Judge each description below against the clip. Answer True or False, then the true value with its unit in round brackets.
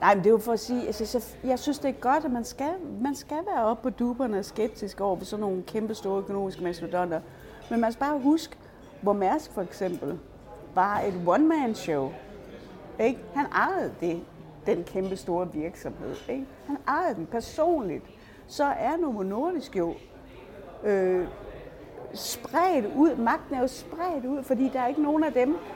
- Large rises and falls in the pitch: True (6.7 semitones)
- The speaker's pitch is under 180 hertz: False (235 Hz)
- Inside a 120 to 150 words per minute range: False (180 wpm)